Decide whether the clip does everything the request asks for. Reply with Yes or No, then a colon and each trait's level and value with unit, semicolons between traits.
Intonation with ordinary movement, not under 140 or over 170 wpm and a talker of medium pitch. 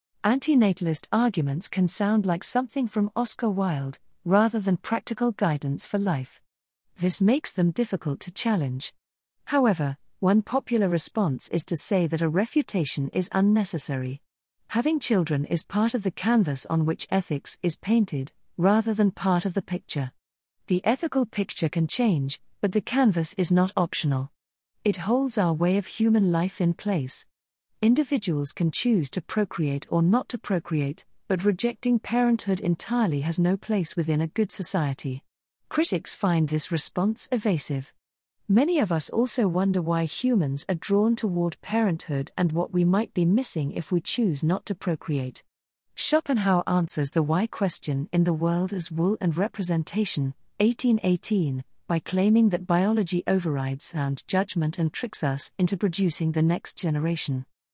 Yes: average, 5.0 semitones; average, 155 wpm; medium, 180 Hz